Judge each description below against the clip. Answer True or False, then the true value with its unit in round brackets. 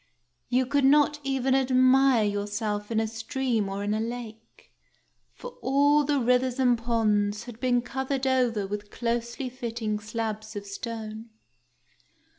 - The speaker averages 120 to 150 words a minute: True (140 wpm)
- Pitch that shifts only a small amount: False (3.3 semitones)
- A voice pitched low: False (235 Hz)